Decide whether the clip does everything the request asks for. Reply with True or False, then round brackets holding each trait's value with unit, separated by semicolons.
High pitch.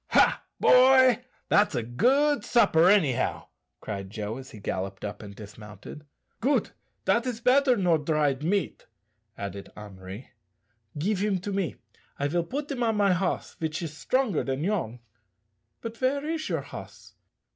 False (170 Hz)